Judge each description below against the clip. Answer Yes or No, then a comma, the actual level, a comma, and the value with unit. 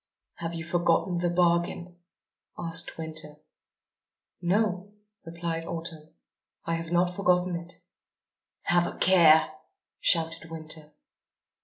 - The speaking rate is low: Yes, slow, 105 wpm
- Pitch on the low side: No, medium, 170 Hz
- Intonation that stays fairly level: Yes, narrow, 1.3 semitones